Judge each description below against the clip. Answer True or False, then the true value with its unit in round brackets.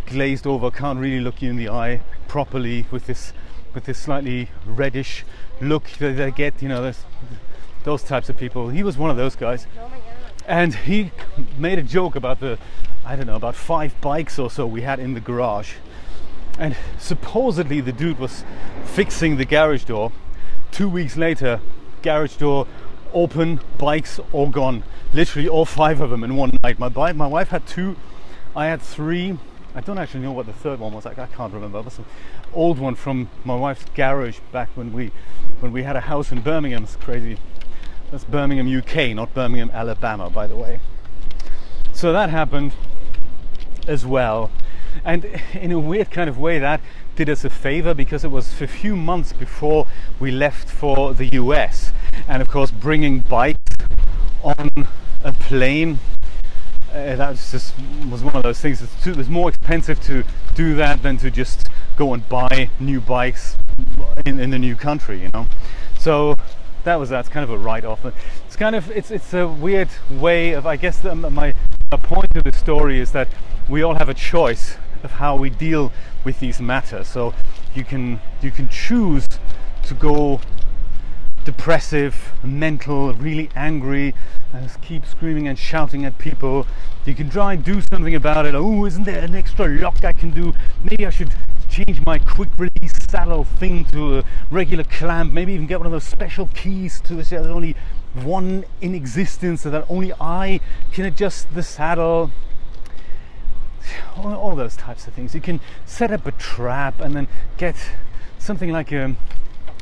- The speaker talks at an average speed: True (180 wpm)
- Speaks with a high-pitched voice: False (140 Hz)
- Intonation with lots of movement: False (4.8 semitones)